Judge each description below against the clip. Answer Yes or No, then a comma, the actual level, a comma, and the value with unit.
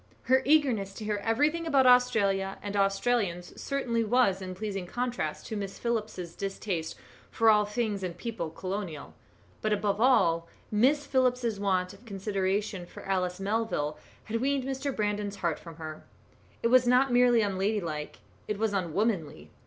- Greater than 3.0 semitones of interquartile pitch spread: Yes, average, 4.3 semitones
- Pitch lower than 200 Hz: No, high, 210 Hz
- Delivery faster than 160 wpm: No, average, 155 wpm